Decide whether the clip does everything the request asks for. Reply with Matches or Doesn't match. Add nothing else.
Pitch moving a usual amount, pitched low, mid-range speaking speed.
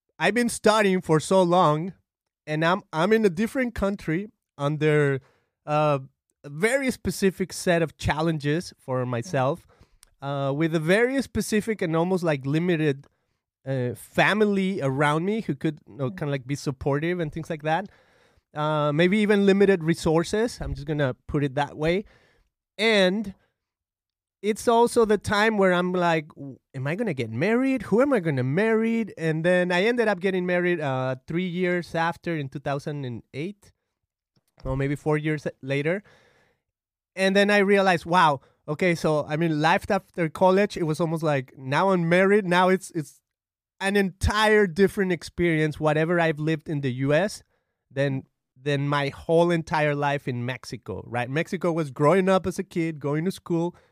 Doesn't match